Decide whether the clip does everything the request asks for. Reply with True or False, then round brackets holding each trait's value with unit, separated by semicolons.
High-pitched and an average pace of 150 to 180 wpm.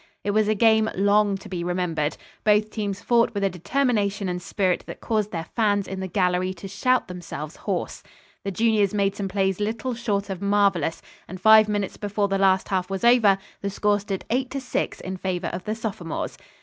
False (200 Hz; 200 wpm)